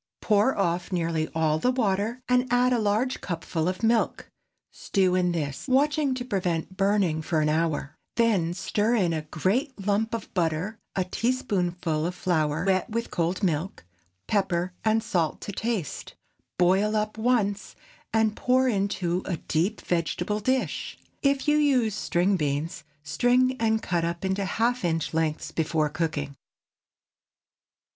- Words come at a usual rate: Yes, average, 150 wpm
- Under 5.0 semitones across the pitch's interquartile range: No, wide, 5.4 semitones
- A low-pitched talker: No, high, 190 Hz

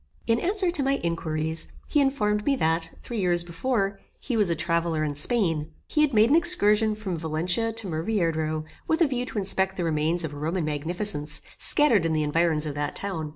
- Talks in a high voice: No, medium, 175 Hz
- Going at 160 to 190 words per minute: No, average, 200 wpm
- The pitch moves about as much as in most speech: No, wide, 6.1 semitones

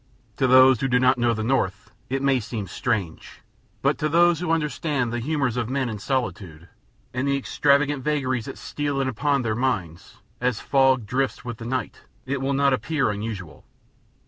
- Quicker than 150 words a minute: Yes, average, 185 wpm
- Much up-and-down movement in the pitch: No, average, 3.4 semitones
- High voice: No, low, 130 Hz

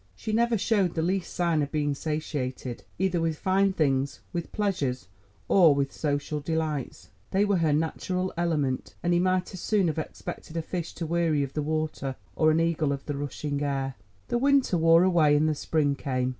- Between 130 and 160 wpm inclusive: No, average, 195 wpm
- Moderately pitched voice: Yes, medium, 160 Hz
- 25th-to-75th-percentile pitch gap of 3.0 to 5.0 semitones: Yes, average, 3.8 semitones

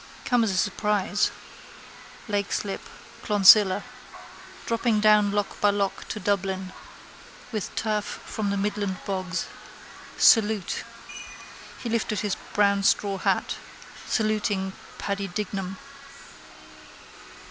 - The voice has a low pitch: No, high, 205 Hz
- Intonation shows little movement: Yes, narrow, 1.4 semitones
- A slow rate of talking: Yes, slow, 100 wpm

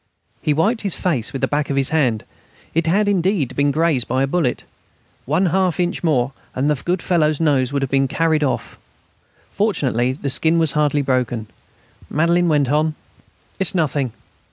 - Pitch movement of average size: Yes, average, 3.8 semitones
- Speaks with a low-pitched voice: No, medium, 150 Hz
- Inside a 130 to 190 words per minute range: Yes, average, 180 wpm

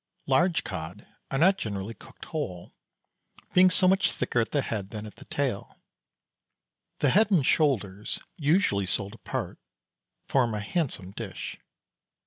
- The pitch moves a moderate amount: No, wide, 8.3 semitones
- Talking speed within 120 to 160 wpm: Yes, average, 140 wpm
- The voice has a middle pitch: No, low, 125 Hz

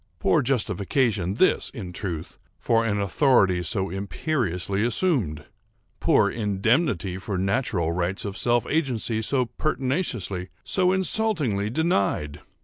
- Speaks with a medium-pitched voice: No, low, 105 Hz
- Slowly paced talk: Yes, slow, 115 wpm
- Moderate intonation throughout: No, wide, 5.9 semitones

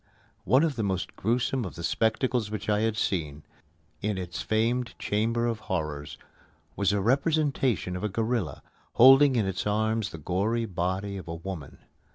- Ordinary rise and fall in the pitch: Yes, average, 3.9 semitones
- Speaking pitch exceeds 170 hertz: No, low, 105 Hz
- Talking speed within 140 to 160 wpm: No, average, 170 wpm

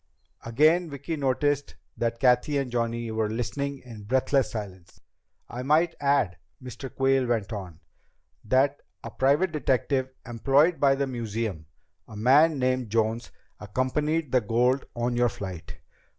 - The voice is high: No, low, 125 Hz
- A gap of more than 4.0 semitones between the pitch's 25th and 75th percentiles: No, average, 3.7 semitones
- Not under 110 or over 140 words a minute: Yes, slow, 135 wpm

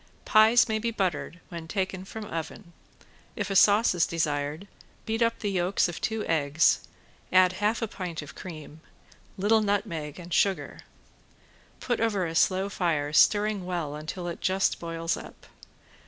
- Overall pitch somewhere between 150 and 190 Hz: Yes, medium, 185 Hz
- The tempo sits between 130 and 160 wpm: Yes, average, 155 wpm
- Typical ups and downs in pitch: Yes, average, 3.9 semitones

